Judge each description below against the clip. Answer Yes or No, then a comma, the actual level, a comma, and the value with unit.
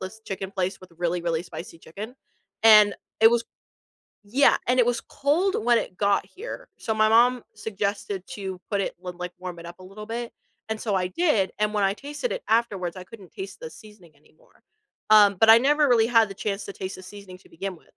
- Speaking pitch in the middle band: No, high, 210 Hz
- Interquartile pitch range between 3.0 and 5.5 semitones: Yes, average, 3.8 semitones